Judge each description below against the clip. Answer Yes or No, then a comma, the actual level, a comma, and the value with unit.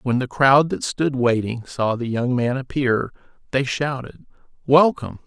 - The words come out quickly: No, average, 160 wpm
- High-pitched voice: No, low, 130 Hz